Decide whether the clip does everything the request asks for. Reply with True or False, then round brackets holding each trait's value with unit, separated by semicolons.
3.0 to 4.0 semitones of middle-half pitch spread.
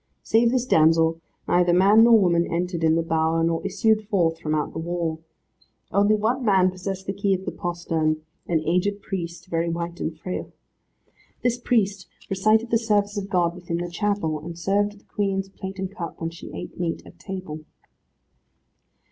True (3.4 semitones)